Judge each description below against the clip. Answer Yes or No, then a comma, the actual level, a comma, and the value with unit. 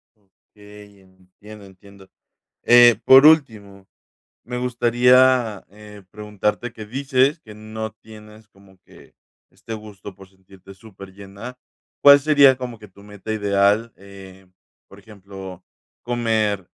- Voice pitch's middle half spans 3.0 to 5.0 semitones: Yes, average, 3.3 semitones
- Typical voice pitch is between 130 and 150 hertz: No, low, 105 Hz